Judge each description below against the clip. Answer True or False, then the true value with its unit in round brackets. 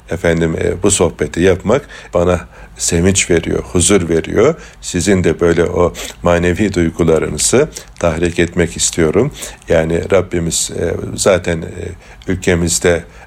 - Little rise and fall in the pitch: True (1.2 semitones)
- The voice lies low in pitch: True (85 Hz)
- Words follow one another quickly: False (115 wpm)